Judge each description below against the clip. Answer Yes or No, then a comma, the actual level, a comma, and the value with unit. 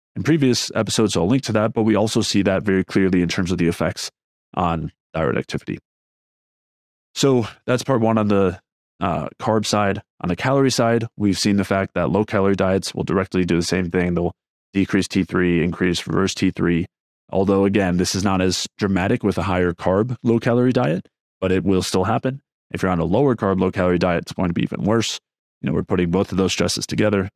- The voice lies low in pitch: Yes, very low, 95 Hz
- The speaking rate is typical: No, fast, 215 wpm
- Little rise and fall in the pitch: No, average, 3.6 semitones